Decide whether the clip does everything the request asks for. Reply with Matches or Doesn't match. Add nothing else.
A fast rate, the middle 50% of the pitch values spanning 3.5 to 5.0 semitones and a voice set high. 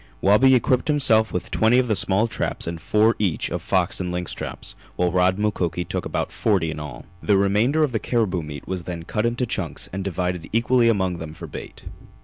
Doesn't match